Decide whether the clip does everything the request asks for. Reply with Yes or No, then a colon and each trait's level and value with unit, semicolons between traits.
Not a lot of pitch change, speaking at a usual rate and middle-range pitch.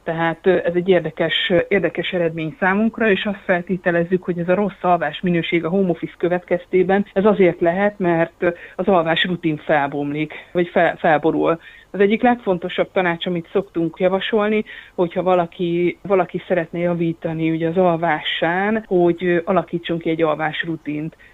Yes: narrow, 2.1 semitones; average, 145 wpm; medium, 175 Hz